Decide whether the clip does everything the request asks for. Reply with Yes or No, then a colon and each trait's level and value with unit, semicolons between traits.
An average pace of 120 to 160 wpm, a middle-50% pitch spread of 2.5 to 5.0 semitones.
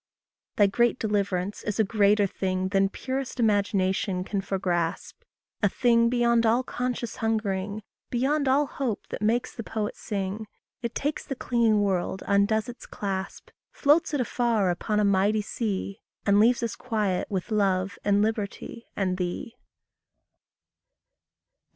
Yes: average, 140 wpm; average, 3.3 semitones